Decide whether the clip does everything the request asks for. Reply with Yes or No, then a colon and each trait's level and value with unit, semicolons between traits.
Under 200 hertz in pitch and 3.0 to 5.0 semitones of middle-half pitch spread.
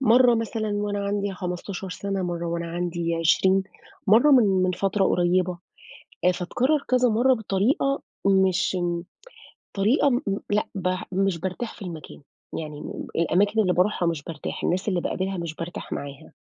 Yes: high, 190 Hz; average, 3.3 semitones